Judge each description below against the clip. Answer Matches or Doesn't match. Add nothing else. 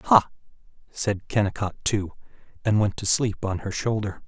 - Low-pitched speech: Matches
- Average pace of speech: Matches